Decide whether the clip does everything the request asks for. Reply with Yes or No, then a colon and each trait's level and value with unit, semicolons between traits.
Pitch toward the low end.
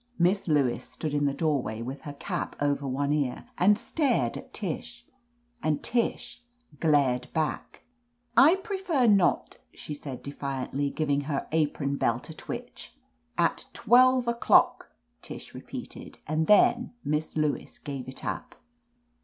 No: medium, 155 Hz